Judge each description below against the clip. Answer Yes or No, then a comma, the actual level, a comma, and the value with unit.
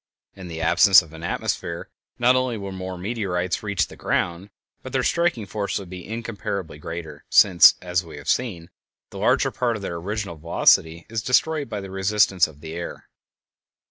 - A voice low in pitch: Yes, very low, 95 Hz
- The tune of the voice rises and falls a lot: No, average, 4.0 semitones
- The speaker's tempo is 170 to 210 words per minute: Yes, average, 180 wpm